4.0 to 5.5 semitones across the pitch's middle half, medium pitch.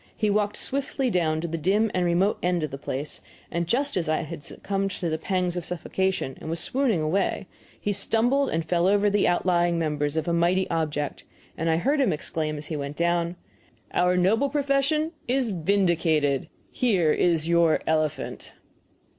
Yes: average, 4.4 semitones; medium, 175 Hz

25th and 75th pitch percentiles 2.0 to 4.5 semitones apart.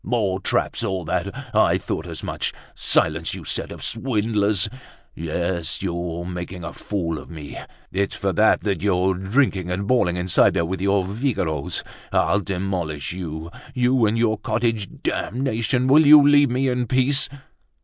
No: average, 5.1 semitones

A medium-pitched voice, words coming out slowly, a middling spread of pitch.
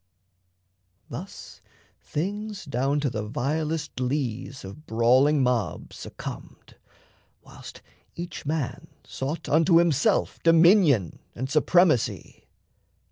Yes: medium, 150 Hz; slow, 90 wpm; average, 4.7 semitones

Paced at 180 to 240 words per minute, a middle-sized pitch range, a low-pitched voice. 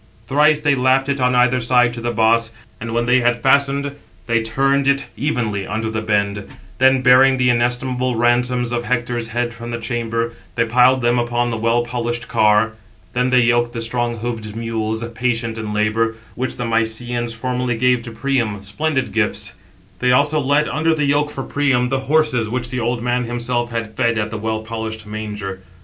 No: average, 190 wpm; narrow, 2.0 semitones; low, 120 Hz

